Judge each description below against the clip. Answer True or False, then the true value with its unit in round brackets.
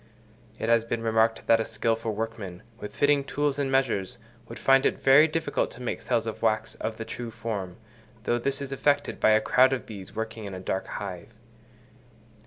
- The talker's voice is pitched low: True (115 Hz)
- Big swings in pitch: False (3.5 semitones)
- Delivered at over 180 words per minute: True (195 wpm)